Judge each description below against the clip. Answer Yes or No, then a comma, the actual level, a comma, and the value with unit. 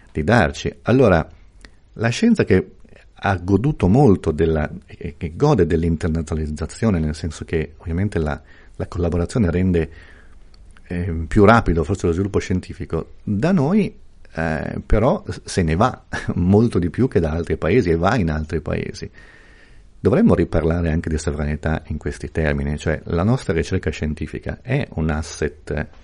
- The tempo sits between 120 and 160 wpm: Yes, average, 145 wpm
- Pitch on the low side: Yes, very low, 85 Hz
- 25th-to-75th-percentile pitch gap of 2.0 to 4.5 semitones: Yes, average, 2.9 semitones